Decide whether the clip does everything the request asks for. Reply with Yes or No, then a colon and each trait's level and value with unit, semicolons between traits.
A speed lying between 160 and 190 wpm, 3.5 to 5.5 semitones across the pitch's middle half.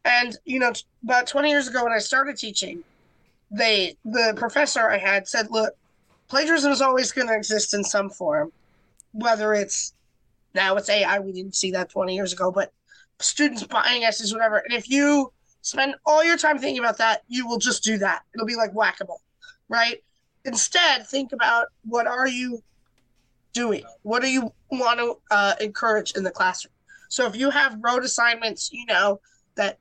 Yes: average, 185 wpm; average, 4.1 semitones